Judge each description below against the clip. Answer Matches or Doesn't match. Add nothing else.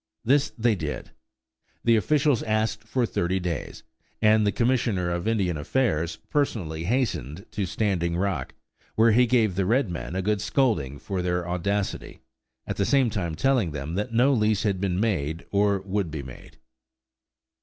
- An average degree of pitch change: Matches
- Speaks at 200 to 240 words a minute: Doesn't match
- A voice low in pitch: Matches